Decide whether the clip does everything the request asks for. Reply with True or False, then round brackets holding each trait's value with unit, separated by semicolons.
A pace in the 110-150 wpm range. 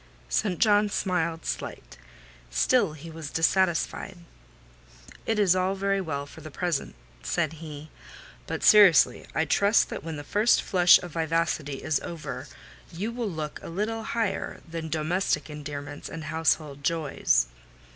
True (145 wpm)